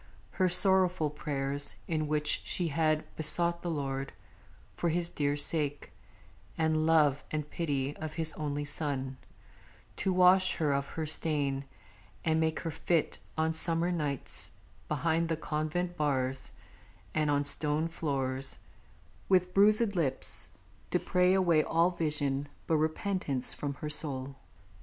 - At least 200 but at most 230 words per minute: No, slow, 135 wpm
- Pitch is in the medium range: Yes, medium, 155 Hz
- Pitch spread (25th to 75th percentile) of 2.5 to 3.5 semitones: Yes, average, 2.9 semitones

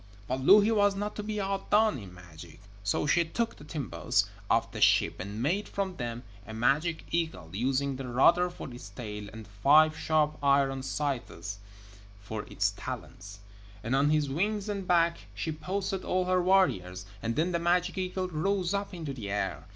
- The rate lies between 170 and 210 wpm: Yes, average, 180 wpm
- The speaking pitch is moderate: Yes, medium, 150 Hz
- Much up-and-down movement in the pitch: Yes, wide, 7.7 semitones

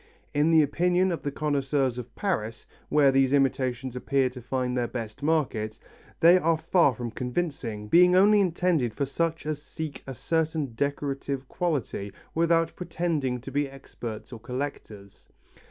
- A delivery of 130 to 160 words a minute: Yes, average, 155 wpm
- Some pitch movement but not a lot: Yes, average, 4.6 semitones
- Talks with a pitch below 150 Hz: Yes, medium, 140 Hz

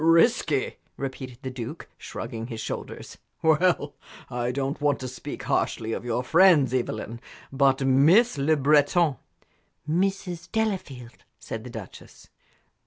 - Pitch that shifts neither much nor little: Yes, average, 4.6 semitones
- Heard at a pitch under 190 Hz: Yes, low, 135 Hz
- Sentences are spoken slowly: Yes, slow, 130 wpm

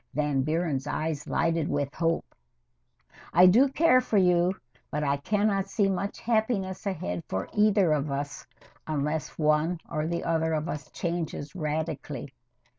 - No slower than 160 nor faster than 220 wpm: No, average, 150 wpm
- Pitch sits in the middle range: Yes, medium, 160 Hz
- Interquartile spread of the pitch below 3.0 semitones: No, average, 4.0 semitones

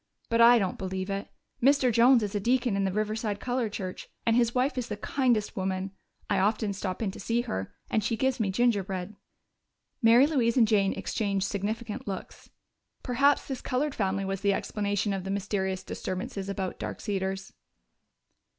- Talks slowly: No, average, 180 wpm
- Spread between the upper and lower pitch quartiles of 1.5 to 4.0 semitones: Yes, average, 3.6 semitones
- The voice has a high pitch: Yes, high, 210 Hz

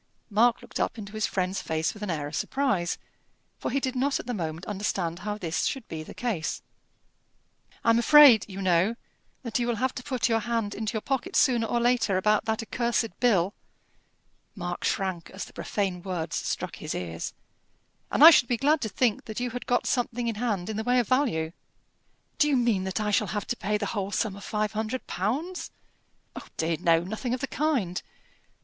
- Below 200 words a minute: No, fast, 205 wpm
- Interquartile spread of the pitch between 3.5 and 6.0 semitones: Yes, average, 4.5 semitones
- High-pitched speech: Yes, high, 215 Hz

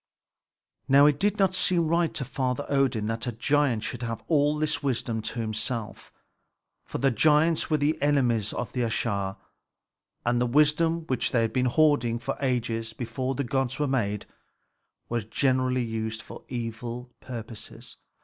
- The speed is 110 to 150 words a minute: No, average, 160 wpm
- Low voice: Yes, low, 125 Hz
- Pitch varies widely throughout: No, average, 4.0 semitones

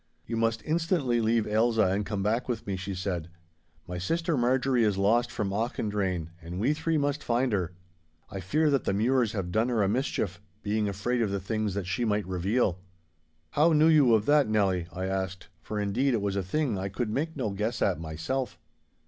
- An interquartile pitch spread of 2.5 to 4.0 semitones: No, average, 4.5 semitones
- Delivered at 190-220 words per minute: Yes, fast, 205 wpm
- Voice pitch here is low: Yes, low, 110 Hz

